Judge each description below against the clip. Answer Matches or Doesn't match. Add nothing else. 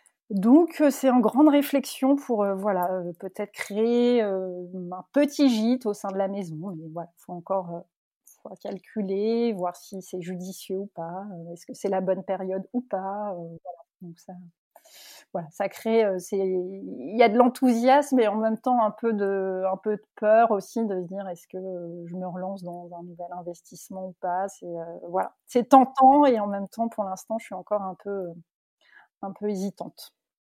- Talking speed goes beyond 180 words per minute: Matches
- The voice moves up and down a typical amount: Matches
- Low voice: Doesn't match